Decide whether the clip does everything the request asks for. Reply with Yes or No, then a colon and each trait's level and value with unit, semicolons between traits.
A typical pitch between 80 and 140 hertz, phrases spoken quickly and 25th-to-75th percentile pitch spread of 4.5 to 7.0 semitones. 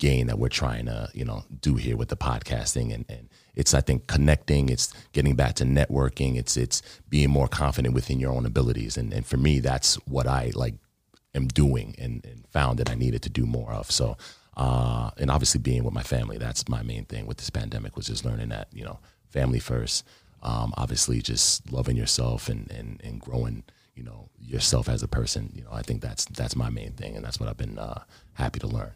No: very low, 65 Hz; fast, 225 wpm; average, 5.2 semitones